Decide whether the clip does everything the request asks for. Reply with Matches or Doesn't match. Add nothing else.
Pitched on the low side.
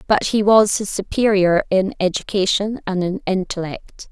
Doesn't match